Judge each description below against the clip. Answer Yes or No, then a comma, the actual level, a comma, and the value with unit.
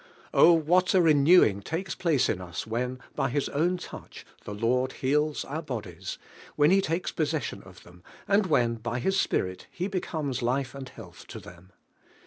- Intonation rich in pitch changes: Yes, wide, 6.2 semitones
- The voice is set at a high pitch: No, medium, 140 Hz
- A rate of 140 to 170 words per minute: No, average, 185 wpm